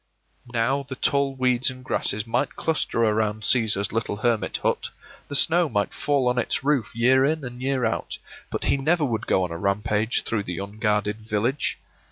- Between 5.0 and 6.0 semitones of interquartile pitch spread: No, average, 4.1 semitones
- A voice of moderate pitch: No, low, 120 Hz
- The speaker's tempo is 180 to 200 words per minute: Yes, average, 185 wpm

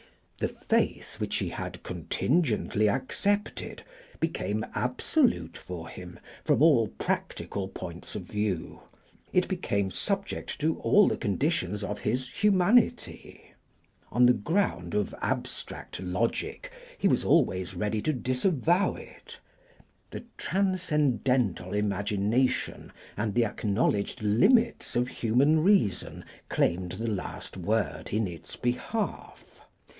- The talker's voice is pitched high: No, low, 115 Hz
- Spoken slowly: Yes, slow, 115 wpm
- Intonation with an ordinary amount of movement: No, wide, 8.1 semitones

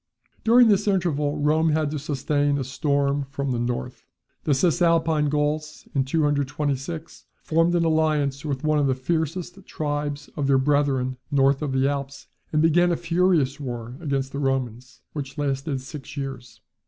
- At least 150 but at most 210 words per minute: Yes, average, 160 wpm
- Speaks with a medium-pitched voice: Yes, medium, 145 Hz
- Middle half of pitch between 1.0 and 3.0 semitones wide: Yes, narrow, 2.5 semitones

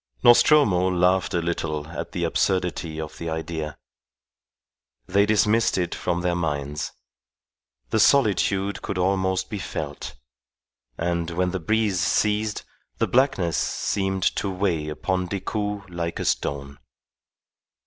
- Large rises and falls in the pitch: No, average, 3.2 semitones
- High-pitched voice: No, very low, 90 Hz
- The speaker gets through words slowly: Yes, slow, 125 wpm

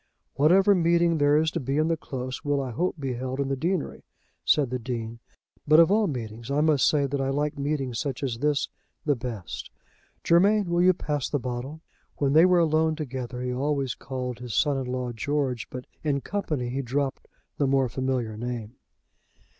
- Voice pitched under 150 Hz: Yes, medium, 140 Hz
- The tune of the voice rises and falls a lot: No, average, 3.7 semitones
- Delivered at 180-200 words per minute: Yes, average, 195 wpm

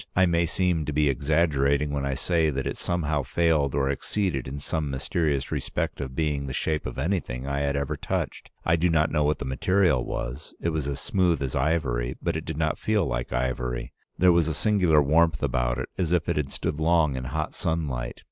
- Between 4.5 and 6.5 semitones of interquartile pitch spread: No, average, 3.5 semitones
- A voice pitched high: No, very low, 75 Hz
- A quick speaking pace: Yes, fast, 215 wpm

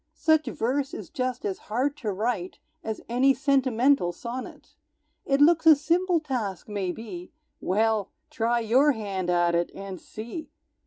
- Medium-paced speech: Yes, average, 145 wpm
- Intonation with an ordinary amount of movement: No, wide, 5.8 semitones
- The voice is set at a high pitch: Yes, high, 235 Hz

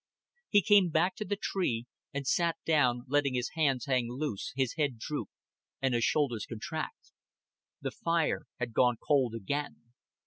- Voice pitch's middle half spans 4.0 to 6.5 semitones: Yes, average, 4.7 semitones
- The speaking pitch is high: No, medium, 140 Hz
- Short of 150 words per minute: No, average, 160 wpm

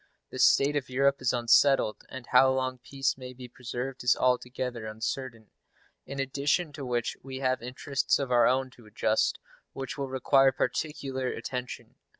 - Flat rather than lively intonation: Yes, narrow, 1.6 semitones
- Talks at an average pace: Yes, average, 160 wpm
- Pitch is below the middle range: Yes, low, 130 Hz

